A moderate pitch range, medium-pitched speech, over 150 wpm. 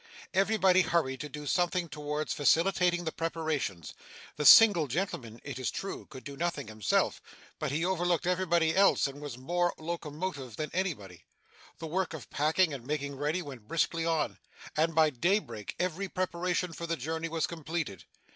Yes: average, 3.7 semitones; medium, 160 Hz; average, 165 wpm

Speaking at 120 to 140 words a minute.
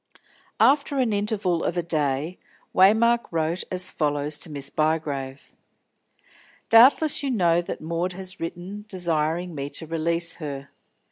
Yes: slow, 135 wpm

